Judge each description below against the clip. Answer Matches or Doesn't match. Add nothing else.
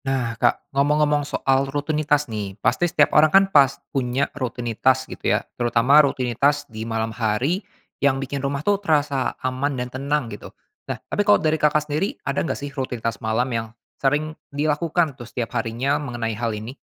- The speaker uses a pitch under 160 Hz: Matches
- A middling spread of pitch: Matches